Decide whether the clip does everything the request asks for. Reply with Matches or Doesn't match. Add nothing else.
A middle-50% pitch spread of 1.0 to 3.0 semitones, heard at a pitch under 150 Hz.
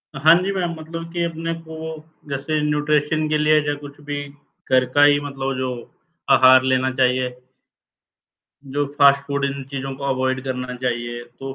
Matches